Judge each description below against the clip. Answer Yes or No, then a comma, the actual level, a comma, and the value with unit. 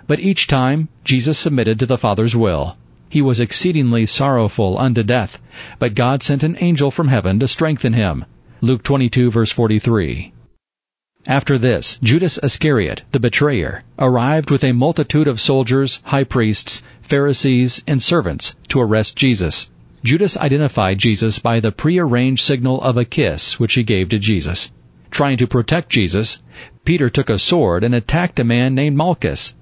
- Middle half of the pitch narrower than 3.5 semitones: No, average, 4.0 semitones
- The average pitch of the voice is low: Yes, low, 125 Hz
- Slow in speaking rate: No, average, 160 wpm